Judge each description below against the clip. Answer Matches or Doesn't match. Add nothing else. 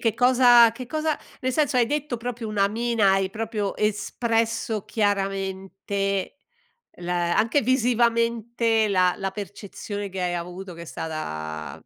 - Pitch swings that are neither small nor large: Matches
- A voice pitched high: Matches